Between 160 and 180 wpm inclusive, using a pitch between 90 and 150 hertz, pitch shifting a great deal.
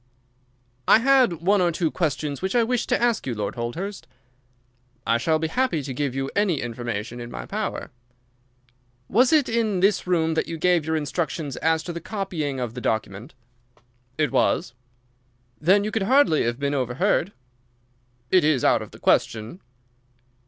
No: average, 170 wpm; medium, 160 Hz; wide, 7.2 semitones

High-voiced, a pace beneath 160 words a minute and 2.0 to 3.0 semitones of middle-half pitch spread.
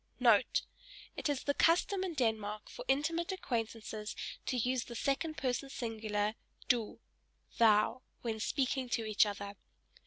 No: high, 240 Hz; slow, 135 wpm; average, 4.2 semitones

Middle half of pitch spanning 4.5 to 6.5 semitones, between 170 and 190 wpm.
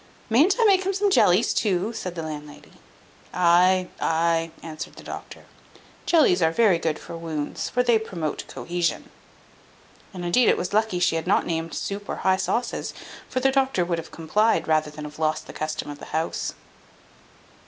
Yes: wide, 5.4 semitones; average, 180 wpm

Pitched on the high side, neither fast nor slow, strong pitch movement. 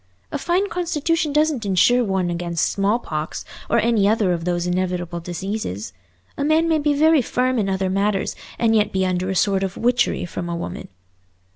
Yes: high, 200 Hz; average, 180 wpm; wide, 6.2 semitones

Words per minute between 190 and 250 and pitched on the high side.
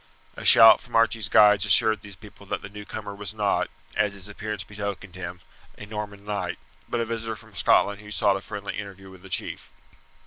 No: average, 200 wpm; low, 105 Hz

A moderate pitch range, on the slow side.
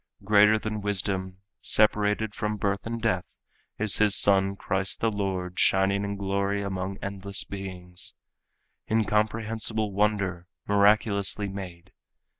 No: narrow, 1.6 semitones; slow, 115 wpm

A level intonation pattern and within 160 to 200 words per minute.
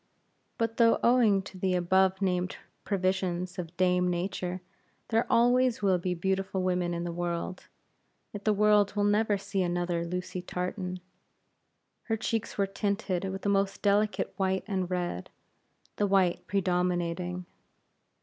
No: narrow, 2.2 semitones; average, 140 wpm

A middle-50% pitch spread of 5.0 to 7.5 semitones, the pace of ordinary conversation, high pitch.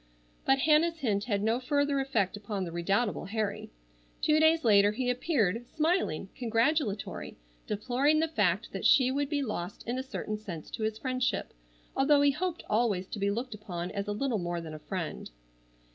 Yes: wide, 5.6 semitones; average, 180 wpm; high, 225 Hz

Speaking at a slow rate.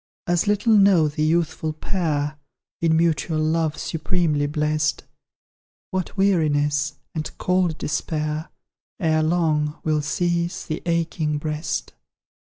Yes: slow, 110 wpm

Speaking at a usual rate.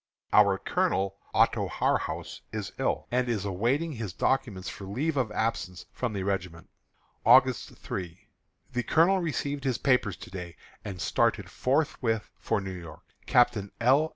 Yes: average, 155 wpm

